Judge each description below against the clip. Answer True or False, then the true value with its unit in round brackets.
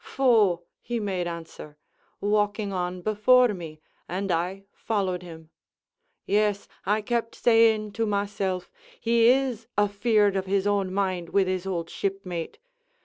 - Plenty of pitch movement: False (2.9 semitones)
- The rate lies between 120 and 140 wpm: True (135 wpm)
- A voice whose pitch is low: False (200 Hz)